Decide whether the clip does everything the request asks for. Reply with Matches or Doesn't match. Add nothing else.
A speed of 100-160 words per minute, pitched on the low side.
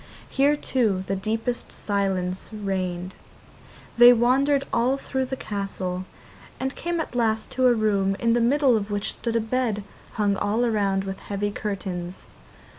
Doesn't match